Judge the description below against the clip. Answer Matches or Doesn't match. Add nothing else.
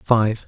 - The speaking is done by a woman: Doesn't match